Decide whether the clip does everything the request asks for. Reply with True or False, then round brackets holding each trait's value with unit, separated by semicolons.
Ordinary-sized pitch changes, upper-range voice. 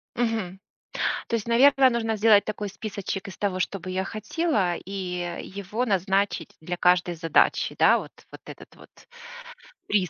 True (3.4 semitones; 195 Hz)